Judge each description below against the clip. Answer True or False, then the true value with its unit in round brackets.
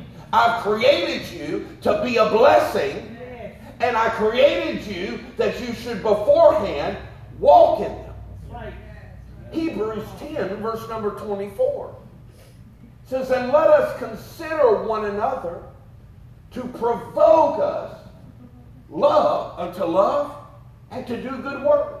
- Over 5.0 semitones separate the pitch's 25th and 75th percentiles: True (5.6 semitones)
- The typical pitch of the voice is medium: False (235 Hz)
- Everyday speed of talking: False (110 wpm)